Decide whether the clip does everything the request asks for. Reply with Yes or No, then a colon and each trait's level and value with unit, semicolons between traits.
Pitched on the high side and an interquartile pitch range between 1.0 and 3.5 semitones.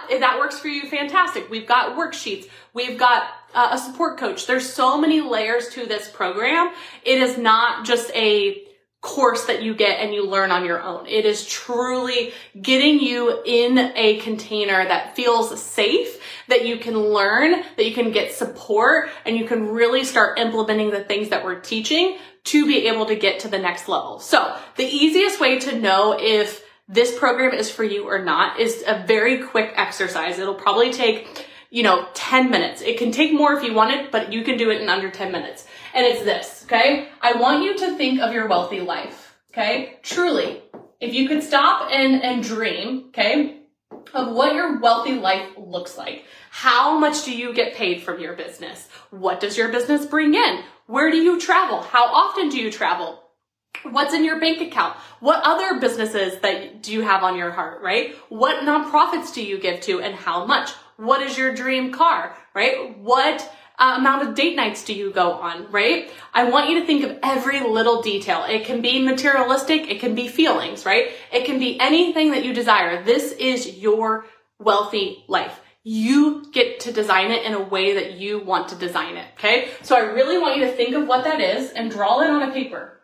No: high, 245 Hz; average, 5.1 semitones